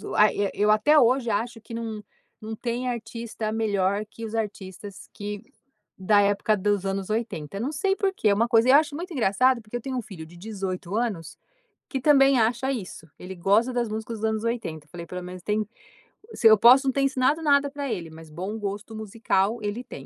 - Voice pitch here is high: Yes, high, 220 Hz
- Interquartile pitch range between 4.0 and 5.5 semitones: No, average, 3.5 semitones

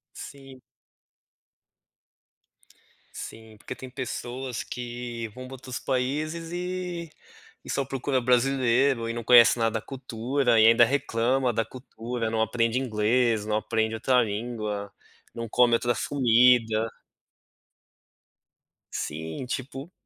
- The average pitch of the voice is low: Yes, low, 120 Hz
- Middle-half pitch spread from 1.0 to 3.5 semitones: Yes, average, 2.7 semitones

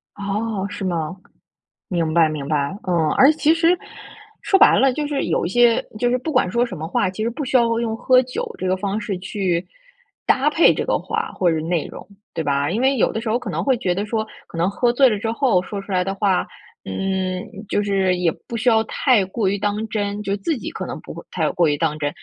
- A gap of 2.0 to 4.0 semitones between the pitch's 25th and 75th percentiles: No, average, 4.8 semitones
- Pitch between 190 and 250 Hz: Yes, high, 200 Hz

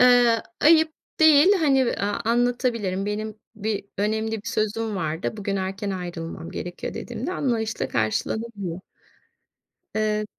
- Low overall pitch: No, high, 215 Hz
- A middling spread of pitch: Yes, average, 3.6 semitones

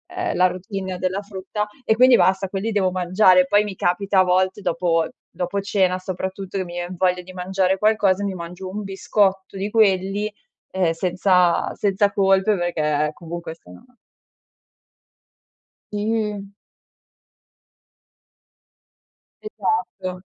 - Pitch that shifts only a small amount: Yes, narrow, 2.0 semitones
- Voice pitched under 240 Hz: Yes, high, 190 Hz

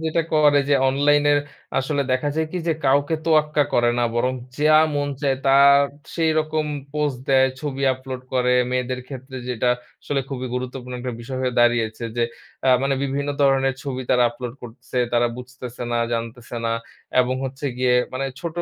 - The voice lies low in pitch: Yes, low, 130 Hz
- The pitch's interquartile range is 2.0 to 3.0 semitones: Yes, narrow, 2.5 semitones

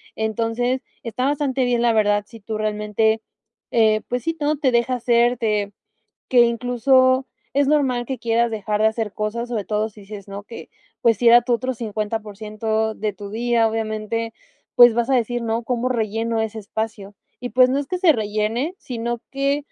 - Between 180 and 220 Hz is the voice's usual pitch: No, high, 230 Hz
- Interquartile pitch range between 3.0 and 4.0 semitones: No, narrow, 2.4 semitones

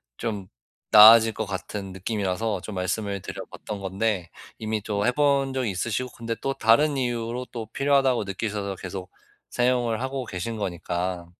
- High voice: No, low, 110 Hz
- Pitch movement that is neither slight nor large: Yes, average, 4.0 semitones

